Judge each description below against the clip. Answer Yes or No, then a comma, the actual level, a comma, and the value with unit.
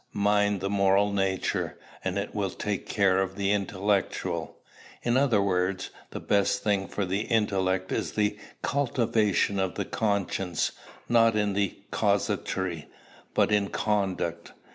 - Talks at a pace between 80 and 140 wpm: Yes, slow, 135 wpm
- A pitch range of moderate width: No, narrow, 1.6 semitones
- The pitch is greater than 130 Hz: No, low, 100 Hz